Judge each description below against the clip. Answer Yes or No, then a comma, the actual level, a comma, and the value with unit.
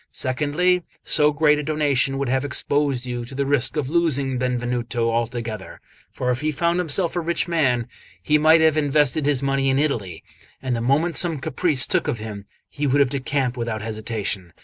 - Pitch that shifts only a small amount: No, average, 3.8 semitones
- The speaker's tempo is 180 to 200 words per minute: Yes, average, 190 wpm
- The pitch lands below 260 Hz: Yes, low, 135 Hz